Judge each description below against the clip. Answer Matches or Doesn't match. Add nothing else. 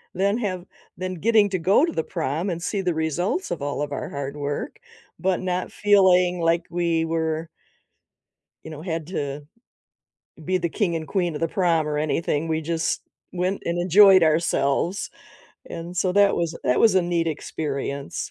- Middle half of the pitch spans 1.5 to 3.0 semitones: Matches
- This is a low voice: Doesn't match